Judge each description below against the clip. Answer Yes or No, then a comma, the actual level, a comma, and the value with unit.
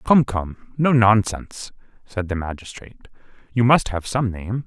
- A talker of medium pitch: No, low, 110 Hz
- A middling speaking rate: Yes, average, 155 wpm